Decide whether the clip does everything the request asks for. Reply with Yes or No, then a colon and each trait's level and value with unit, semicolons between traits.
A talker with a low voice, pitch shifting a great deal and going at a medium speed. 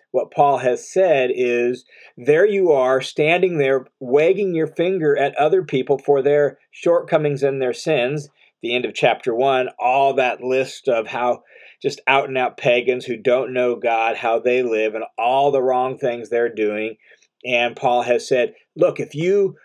No: low, 130 Hz; average, 3.2 semitones; average, 175 wpm